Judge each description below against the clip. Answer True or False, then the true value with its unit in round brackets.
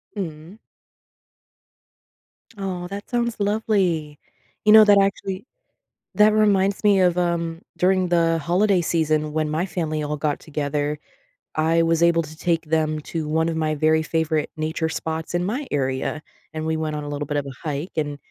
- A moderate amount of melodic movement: True (3.3 semitones)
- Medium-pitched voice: True (165 Hz)